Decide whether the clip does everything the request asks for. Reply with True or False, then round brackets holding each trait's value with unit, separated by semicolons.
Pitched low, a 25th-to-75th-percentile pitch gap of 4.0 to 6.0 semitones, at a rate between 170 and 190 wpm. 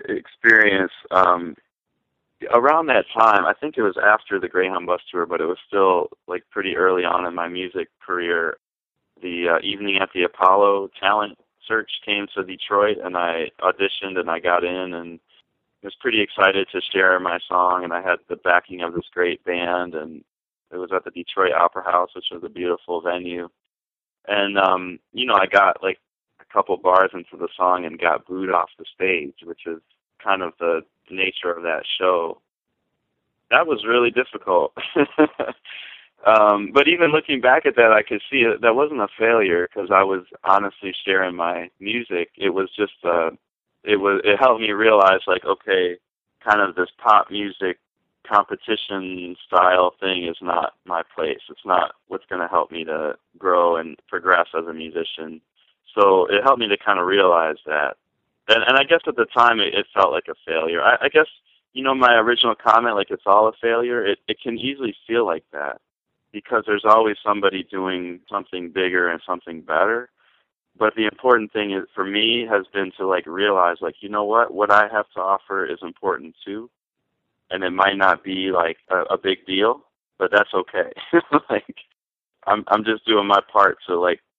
True (95 Hz; 4.5 semitones; 185 wpm)